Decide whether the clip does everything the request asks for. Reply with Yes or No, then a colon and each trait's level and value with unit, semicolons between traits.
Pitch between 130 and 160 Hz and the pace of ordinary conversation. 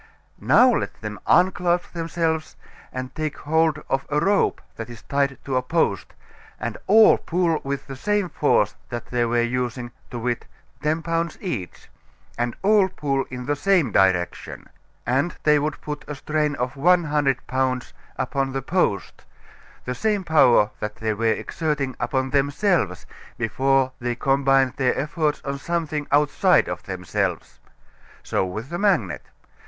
Yes: medium, 140 Hz; average, 155 wpm